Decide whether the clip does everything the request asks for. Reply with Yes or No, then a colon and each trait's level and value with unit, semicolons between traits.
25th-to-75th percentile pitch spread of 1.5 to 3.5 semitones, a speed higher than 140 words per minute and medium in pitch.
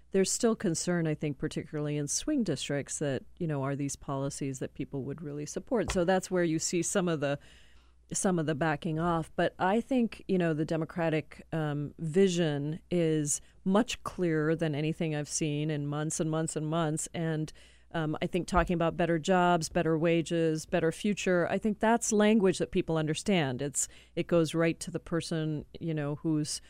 Yes: average, 2.7 semitones; average, 190 wpm; medium, 165 Hz